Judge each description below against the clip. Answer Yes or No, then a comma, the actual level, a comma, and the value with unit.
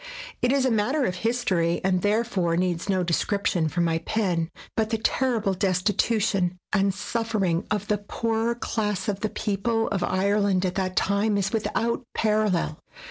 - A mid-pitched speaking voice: No, high, 200 Hz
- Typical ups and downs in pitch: Yes, average, 3.4 semitones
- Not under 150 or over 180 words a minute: Yes, average, 165 wpm